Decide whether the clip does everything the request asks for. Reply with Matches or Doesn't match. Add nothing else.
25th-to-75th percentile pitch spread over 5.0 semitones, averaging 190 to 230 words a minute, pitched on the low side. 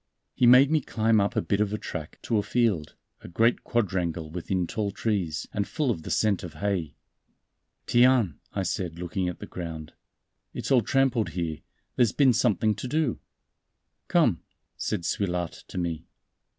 Doesn't match